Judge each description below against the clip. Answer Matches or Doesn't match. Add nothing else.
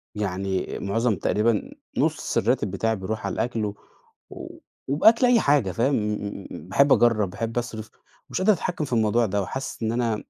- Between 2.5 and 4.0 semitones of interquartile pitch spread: Matches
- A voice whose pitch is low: Matches